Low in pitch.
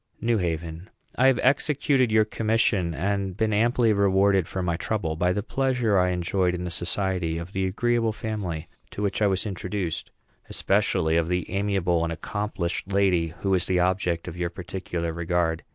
Yes: very low, 95 Hz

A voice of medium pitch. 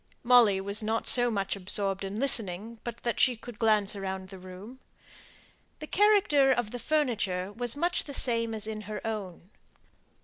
No: high, 220 Hz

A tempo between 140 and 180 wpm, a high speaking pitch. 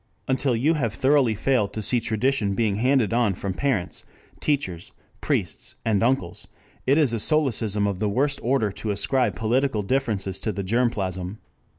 No: average, 170 wpm; low, 115 Hz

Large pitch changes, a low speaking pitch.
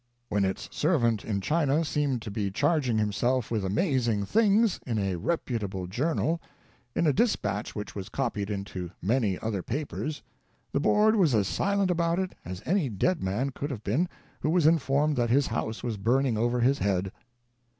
Yes: wide, 6.9 semitones; low, 120 Hz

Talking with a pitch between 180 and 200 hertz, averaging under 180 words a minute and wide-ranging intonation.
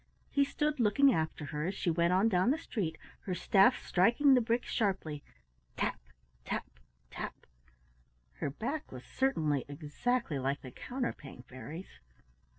Yes: medium, 185 Hz; average, 145 wpm; wide, 8.7 semitones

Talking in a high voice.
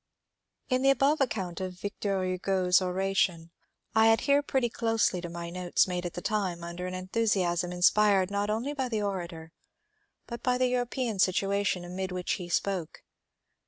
Yes: high, 195 Hz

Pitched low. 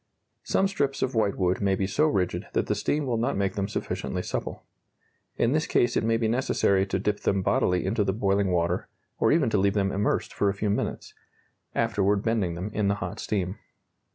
Yes: low, 100 Hz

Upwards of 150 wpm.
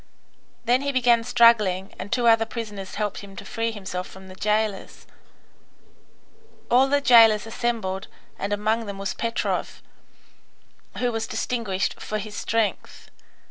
No: average, 140 wpm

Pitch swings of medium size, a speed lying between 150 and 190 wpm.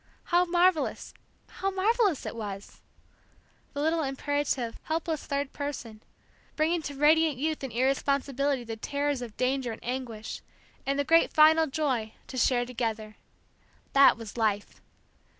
No: average, 4.6 semitones; slow, 135 wpm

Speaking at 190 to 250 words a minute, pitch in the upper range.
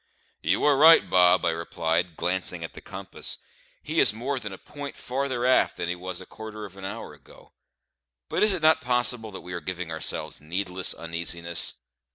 No: average, 195 wpm; very low, 95 Hz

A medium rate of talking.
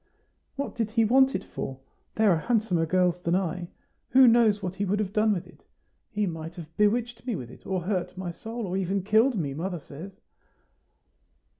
Yes: average, 195 wpm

